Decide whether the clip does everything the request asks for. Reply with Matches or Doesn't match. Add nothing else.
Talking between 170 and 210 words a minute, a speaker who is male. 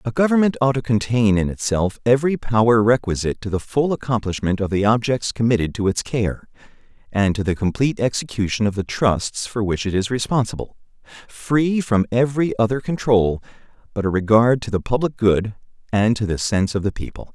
Matches